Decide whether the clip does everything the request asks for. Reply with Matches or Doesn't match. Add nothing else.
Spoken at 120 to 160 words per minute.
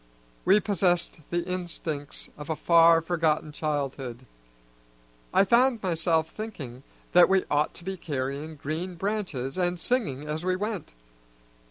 Matches